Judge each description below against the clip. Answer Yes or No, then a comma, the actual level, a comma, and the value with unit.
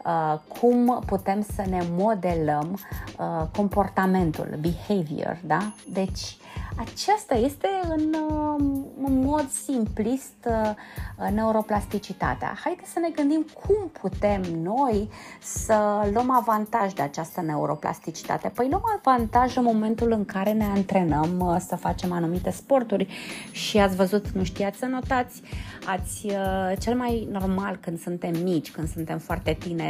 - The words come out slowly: No, average, 135 wpm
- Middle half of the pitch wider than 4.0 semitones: Yes, average, 5.2 semitones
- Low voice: No, high, 205 Hz